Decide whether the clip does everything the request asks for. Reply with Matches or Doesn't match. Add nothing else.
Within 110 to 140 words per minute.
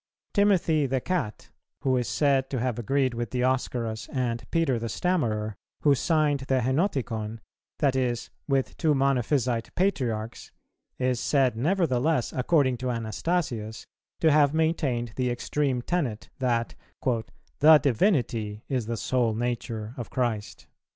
Matches